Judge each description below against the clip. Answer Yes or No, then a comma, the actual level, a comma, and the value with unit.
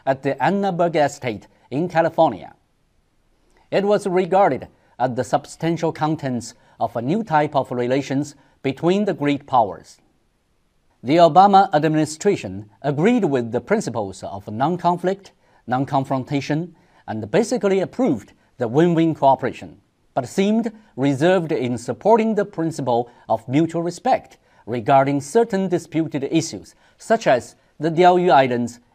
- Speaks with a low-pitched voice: No, medium, 155 Hz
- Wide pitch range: Yes, wide, 5.8 semitones